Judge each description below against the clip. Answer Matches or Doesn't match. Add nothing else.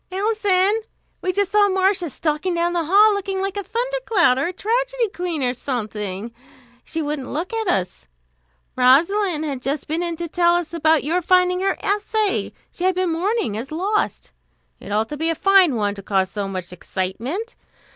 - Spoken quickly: Doesn't match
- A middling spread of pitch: Doesn't match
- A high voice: Matches